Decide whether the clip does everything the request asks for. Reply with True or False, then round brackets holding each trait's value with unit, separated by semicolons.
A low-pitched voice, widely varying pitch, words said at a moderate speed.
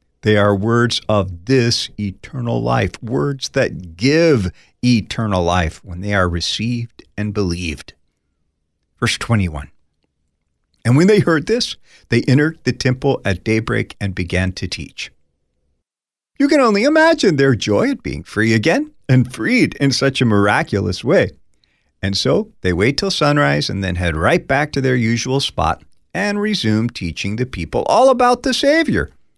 True (105 Hz; 8.2 semitones; 155 wpm)